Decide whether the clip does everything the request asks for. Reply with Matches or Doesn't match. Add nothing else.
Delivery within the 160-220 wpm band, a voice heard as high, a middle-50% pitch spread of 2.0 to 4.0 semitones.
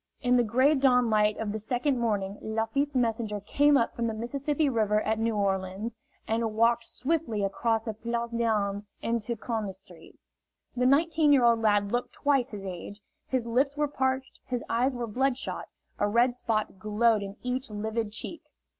Matches